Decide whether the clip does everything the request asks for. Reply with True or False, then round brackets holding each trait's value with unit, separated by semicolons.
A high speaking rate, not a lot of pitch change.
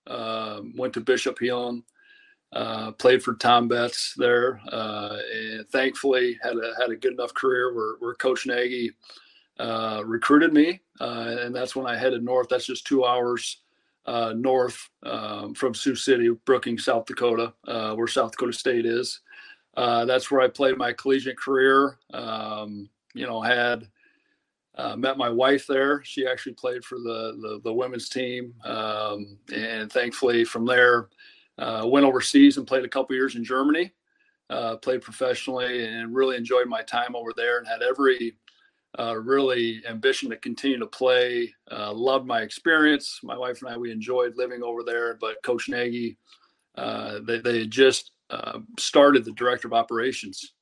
False (165 wpm; 2.3 semitones)